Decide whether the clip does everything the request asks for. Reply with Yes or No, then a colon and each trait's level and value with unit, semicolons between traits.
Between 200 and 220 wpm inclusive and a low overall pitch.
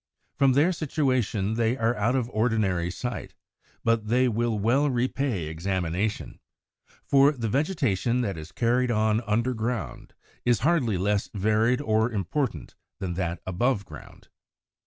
No: slow, 135 wpm; low, 115 Hz